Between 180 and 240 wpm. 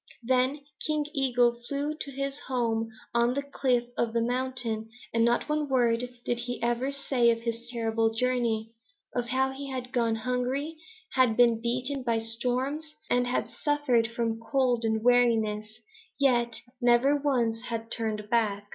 No: average, 155 wpm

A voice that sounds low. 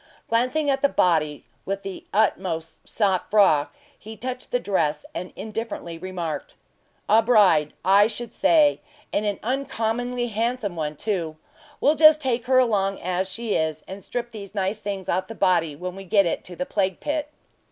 No: high, 205 Hz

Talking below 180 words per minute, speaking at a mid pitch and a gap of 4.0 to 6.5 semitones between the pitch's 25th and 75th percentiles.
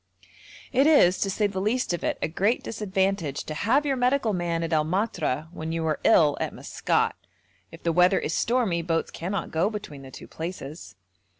No: average, 195 wpm; medium, 180 Hz; average, 4.7 semitones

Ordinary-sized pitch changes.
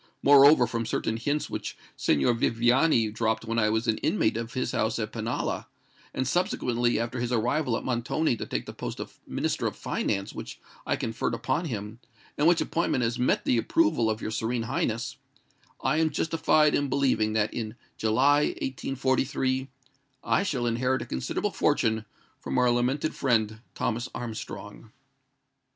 Yes: average, 3.1 semitones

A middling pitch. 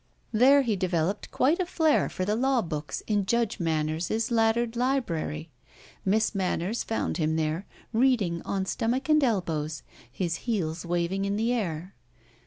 No: high, 200 Hz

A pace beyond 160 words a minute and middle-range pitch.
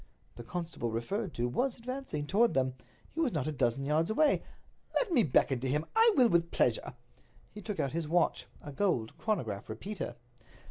Yes: average, 170 wpm; medium, 160 Hz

